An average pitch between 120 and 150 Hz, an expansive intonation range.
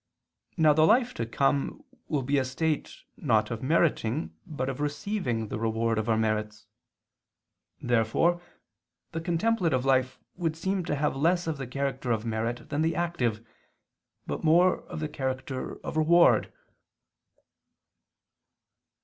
Yes: medium, 140 Hz; wide, 5.8 semitones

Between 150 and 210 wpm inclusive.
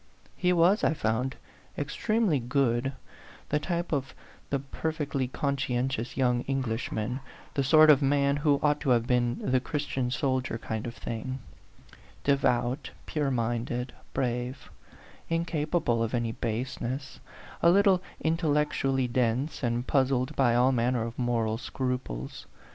No: slow, 135 wpm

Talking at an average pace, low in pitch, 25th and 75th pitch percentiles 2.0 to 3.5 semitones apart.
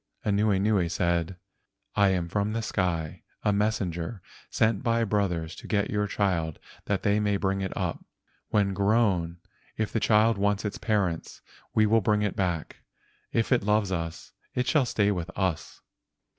Yes: average, 170 wpm; low, 100 Hz; average, 3.0 semitones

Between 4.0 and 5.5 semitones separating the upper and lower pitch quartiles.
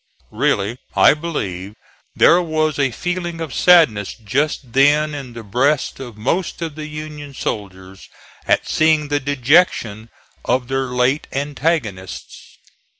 Yes: average, 4.9 semitones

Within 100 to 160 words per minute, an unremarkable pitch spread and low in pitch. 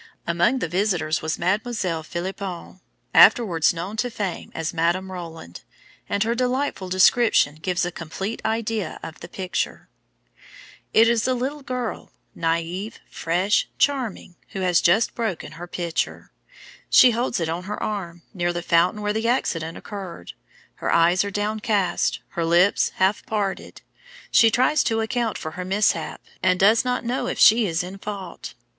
No: average, 155 wpm; average, 4.4 semitones; high, 190 Hz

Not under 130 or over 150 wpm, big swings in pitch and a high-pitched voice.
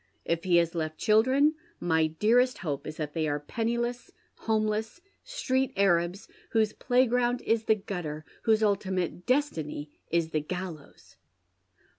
Yes: slow, 135 wpm; wide, 6.4 semitones; high, 195 Hz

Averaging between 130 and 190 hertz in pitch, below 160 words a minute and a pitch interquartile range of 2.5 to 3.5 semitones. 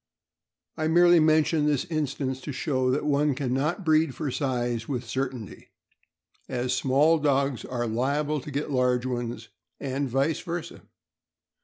Yes: medium, 140 Hz; average, 145 wpm; average, 3.1 semitones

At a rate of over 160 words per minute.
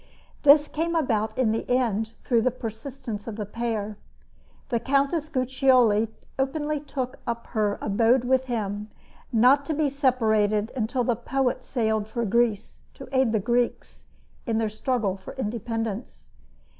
No: average, 145 wpm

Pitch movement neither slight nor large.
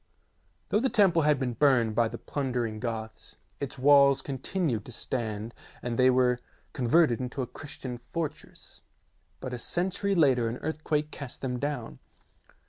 Yes: average, 3.8 semitones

